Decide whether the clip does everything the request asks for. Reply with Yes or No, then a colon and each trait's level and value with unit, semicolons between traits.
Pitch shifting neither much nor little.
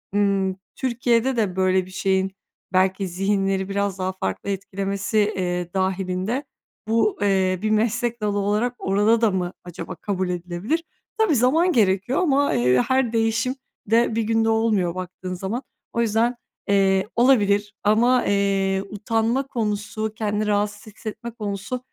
Yes: average, 3.2 semitones